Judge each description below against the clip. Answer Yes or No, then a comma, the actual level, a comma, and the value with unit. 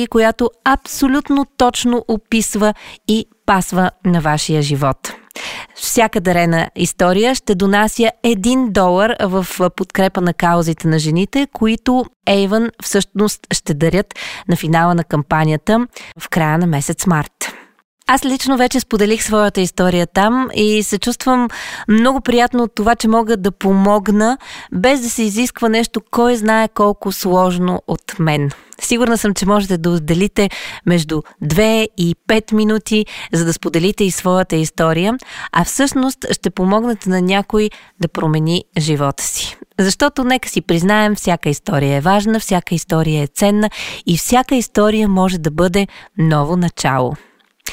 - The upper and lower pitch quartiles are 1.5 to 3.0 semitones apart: No, average, 4.6 semitones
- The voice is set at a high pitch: Yes, high, 205 Hz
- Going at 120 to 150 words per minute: Yes, average, 140 wpm